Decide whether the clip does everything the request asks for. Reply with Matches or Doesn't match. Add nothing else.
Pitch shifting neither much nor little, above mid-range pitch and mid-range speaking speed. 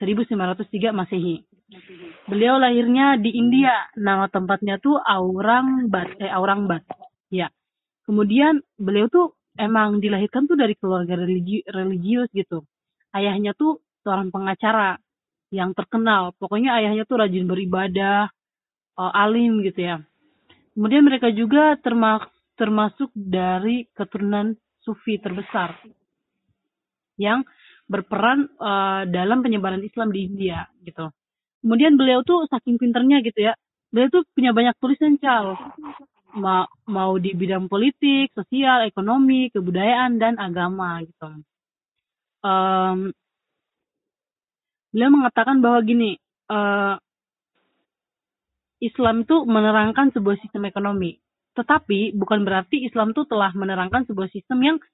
Matches